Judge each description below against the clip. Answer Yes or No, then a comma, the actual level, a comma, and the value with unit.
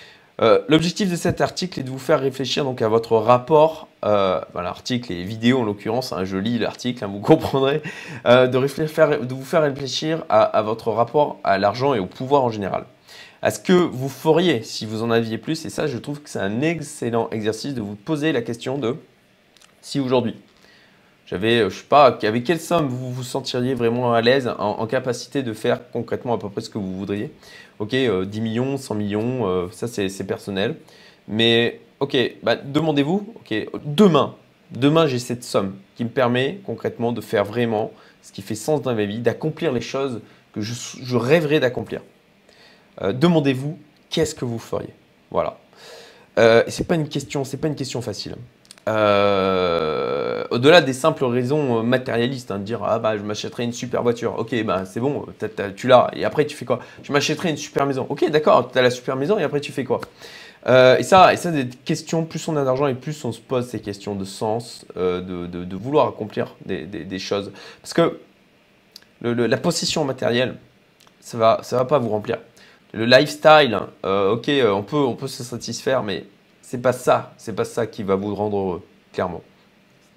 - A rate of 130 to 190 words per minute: No, average, 205 wpm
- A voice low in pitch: Yes, low, 125 Hz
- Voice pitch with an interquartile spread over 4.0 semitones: Yes, average, 4.9 semitones